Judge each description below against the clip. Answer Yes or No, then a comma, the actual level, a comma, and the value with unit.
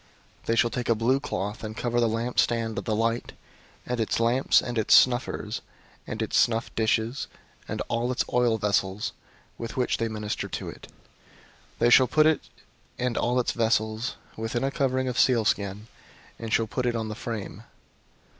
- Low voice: Yes, low, 115 Hz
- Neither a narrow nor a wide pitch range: No, narrow, 2.0 semitones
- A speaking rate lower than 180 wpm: No, average, 185 wpm